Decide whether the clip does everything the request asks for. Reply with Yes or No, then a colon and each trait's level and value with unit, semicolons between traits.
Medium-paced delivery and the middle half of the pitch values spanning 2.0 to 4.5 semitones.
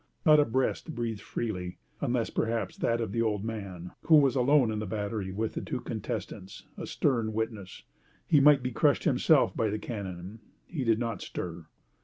Yes: average, 185 wpm; average, 3.6 semitones